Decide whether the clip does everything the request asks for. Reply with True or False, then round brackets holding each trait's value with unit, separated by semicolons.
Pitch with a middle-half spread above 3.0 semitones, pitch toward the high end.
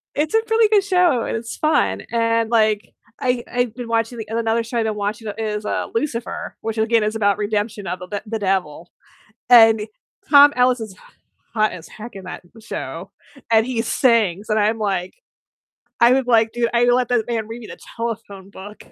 False (2.4 semitones; 225 Hz)